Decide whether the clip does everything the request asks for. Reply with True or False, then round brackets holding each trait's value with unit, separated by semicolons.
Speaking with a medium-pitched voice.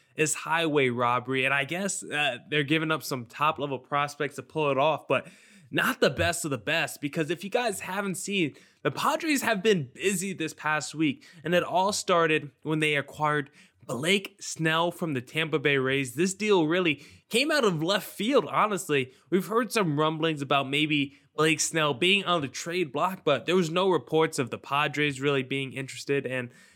True (155 Hz)